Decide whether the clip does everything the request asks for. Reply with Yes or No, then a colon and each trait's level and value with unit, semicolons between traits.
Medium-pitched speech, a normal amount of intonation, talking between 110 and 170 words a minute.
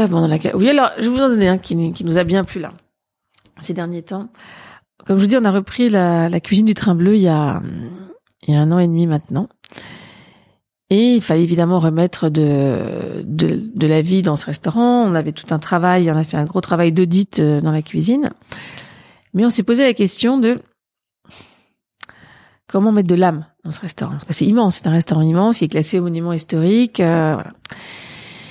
No: medium, 180 Hz; average, 4.2 semitones; average, 215 wpm